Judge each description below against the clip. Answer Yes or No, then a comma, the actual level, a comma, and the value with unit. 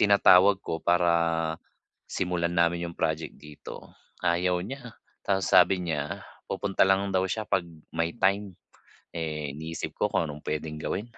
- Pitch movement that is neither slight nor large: Yes, average, 3.0 semitones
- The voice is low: Yes, very low, 85 Hz